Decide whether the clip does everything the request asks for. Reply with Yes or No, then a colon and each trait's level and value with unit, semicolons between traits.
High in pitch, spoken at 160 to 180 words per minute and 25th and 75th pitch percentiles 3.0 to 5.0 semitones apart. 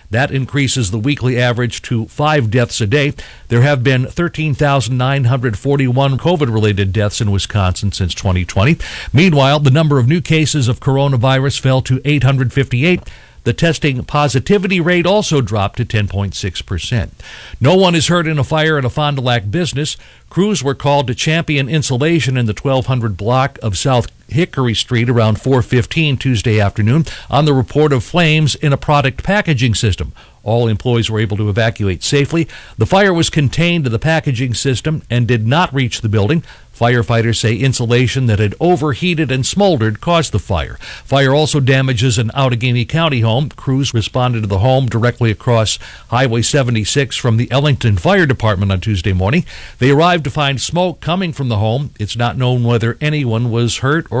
No: low, 130 Hz; average, 170 wpm; average, 4.3 semitones